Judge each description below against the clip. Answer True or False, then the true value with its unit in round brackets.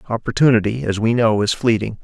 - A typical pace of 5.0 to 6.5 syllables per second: True (6.0 syllables/s)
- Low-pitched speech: True (115 Hz)